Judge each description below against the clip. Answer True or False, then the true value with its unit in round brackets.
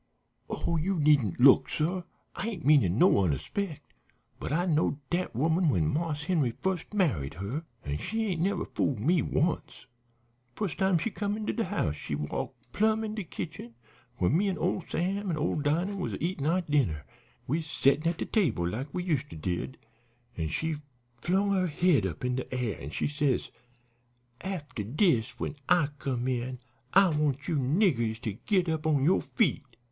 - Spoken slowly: False (185 wpm)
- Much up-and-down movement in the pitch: True (6.5 semitones)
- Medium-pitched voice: True (155 Hz)